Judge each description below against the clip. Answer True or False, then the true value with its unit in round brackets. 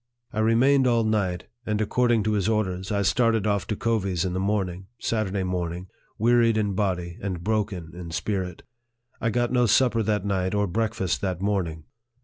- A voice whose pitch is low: True (100 Hz)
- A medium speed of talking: True (180 wpm)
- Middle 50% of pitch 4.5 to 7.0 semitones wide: False (3.3 semitones)